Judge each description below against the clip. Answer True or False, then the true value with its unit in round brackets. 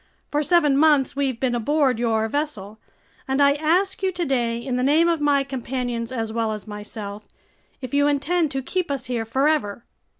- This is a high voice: True (270 Hz)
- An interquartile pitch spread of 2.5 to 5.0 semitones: True (4.2 semitones)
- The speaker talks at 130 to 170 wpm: False (180 wpm)